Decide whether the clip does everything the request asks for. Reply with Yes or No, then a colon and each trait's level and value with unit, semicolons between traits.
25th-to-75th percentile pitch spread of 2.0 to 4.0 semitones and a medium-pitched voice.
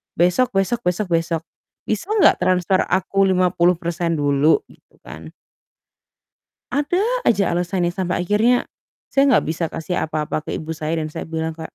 Yes: average, 3.2 semitones; medium, 175 Hz